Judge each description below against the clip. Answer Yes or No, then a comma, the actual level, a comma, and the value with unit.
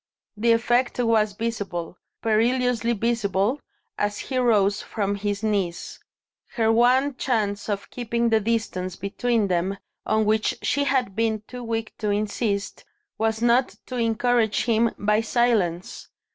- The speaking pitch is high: Yes, high, 225 Hz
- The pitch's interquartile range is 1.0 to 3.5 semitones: Yes, narrow, 2.6 semitones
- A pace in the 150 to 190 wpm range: No, slow, 135 wpm